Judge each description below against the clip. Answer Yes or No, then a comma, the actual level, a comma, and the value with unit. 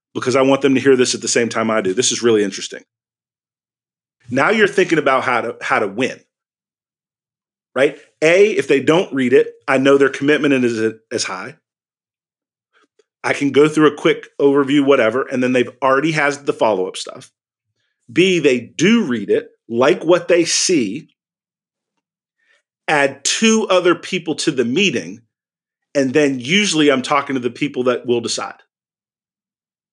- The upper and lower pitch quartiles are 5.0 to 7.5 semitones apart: Yes, wide, 5.6 semitones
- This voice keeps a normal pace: Yes, average, 170 wpm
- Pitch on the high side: No, medium, 140 Hz